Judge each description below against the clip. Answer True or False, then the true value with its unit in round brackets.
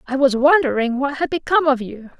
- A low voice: False (275 Hz)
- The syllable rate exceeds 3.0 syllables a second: True (6.0 syllables/s)